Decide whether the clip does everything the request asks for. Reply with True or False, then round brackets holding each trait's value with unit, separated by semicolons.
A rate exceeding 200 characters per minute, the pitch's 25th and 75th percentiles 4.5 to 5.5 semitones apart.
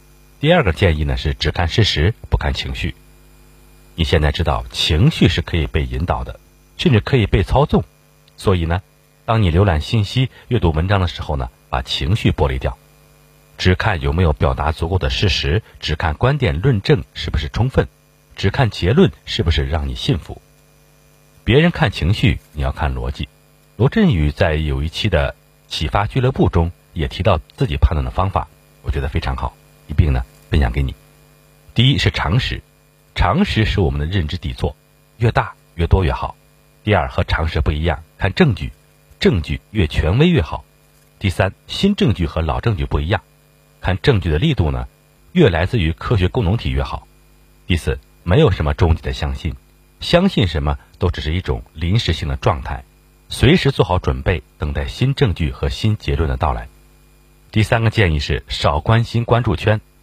True (265 characters per minute; 5.1 semitones)